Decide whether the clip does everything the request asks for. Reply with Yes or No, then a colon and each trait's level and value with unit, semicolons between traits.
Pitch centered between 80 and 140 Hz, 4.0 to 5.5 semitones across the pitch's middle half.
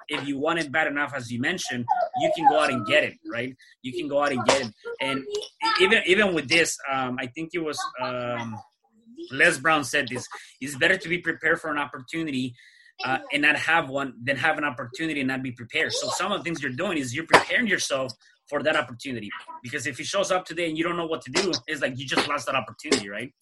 No: medium, 155 Hz; average, 4.7 semitones